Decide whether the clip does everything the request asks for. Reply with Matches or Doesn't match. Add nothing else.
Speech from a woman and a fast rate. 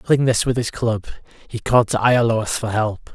Doesn't match